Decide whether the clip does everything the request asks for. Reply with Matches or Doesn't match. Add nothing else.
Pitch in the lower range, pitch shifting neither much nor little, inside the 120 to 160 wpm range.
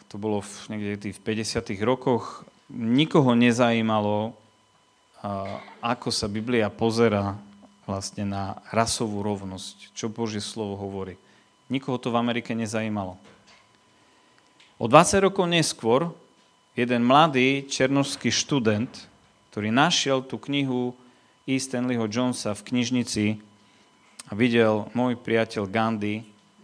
Doesn't match